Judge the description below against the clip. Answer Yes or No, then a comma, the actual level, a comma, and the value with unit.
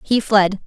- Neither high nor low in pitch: No, high, 205 Hz